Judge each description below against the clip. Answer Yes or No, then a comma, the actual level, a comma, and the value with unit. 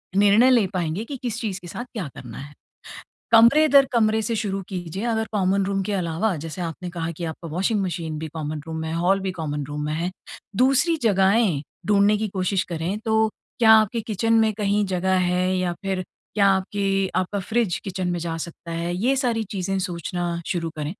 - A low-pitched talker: No, high, 190 Hz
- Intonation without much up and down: No, average, 4.0 semitones